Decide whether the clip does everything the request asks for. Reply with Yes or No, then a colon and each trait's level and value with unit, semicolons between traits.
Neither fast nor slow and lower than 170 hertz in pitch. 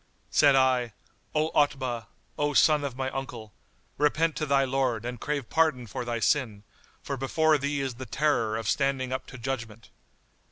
Yes: average, 170 wpm; low, 135 Hz